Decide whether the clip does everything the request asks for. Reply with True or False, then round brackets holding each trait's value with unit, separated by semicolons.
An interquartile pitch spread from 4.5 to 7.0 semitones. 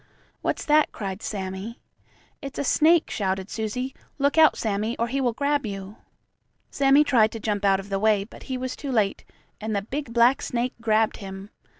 True (5.0 semitones)